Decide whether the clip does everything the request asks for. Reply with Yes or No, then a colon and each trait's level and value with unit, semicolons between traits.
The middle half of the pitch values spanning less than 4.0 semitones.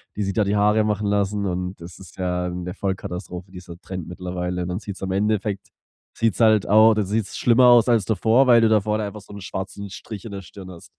Yes: average, 2.8 semitones